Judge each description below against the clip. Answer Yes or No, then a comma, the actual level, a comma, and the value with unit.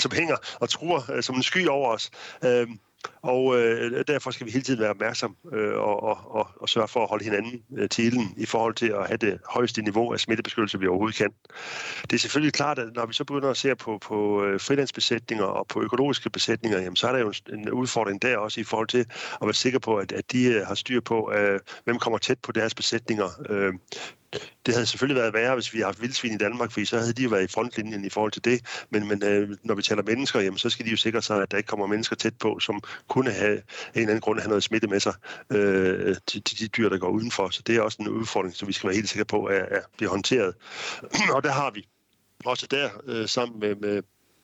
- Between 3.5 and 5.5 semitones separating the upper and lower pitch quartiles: No, narrow, 2.6 semitones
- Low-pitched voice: Yes, low, 115 Hz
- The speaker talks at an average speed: No, fast, 240 wpm